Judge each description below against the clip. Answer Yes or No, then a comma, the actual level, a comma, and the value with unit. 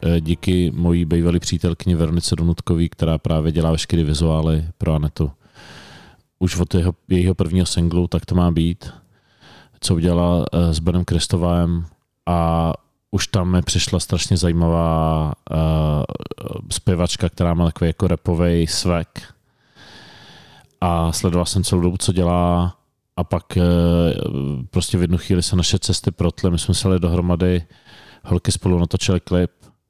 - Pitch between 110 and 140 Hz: No, very low, 85 Hz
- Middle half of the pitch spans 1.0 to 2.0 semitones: Yes, narrow, 1.4 semitones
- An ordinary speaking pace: Yes, average, 135 wpm